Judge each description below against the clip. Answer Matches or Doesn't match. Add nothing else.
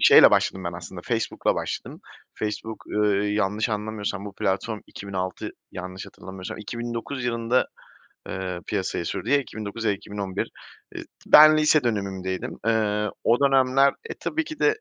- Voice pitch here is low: Matches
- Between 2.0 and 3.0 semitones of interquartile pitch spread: Doesn't match